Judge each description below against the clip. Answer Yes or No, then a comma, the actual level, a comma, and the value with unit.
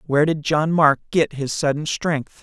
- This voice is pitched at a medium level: Yes, medium, 150 Hz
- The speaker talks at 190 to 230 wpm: Yes, average, 200 wpm